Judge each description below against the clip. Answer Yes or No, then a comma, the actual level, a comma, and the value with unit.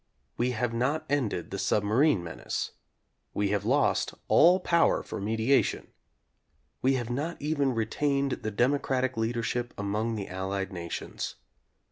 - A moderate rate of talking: No, slow, 130 wpm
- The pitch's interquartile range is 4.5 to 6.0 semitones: Yes, average, 5.1 semitones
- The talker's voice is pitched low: Yes, low, 120 Hz